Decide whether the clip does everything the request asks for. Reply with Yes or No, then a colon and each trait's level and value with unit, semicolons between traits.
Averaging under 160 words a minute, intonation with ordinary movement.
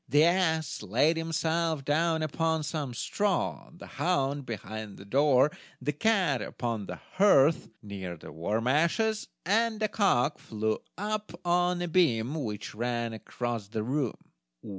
No: average, 140 wpm; wide, 6.6 semitones